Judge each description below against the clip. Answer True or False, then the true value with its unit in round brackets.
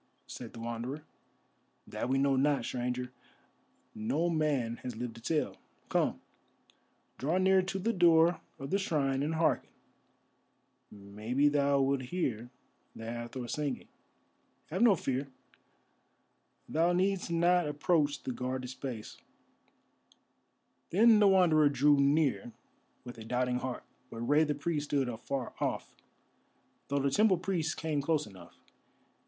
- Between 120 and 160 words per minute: True (135 wpm)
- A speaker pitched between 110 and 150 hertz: True (140 Hz)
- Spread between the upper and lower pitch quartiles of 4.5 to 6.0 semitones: True (4.8 semitones)